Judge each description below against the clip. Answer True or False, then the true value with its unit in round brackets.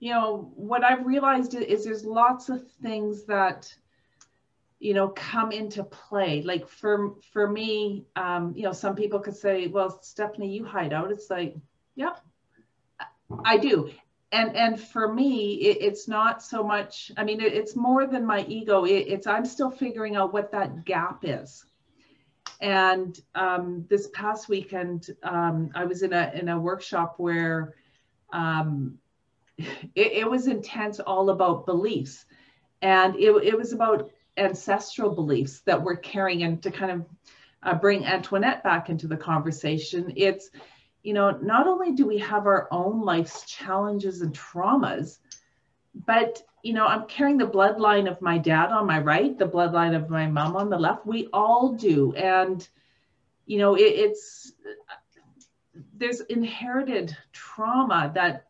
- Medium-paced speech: True (160 wpm)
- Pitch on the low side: False (200 Hz)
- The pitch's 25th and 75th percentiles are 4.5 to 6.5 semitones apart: False (4.0 semitones)